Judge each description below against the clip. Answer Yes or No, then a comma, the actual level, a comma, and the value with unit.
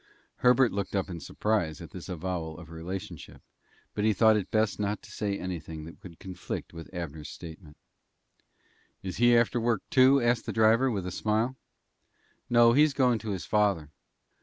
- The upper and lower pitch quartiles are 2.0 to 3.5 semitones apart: No, average, 5.1 semitones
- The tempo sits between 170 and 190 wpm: Yes, average, 175 wpm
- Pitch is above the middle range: No, low, 100 Hz